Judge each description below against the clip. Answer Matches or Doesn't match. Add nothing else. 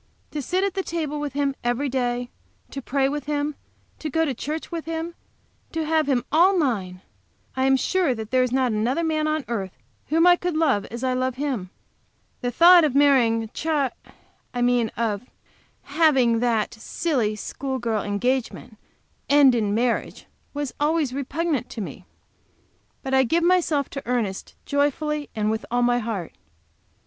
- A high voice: Matches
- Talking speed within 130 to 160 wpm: Doesn't match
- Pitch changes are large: Doesn't match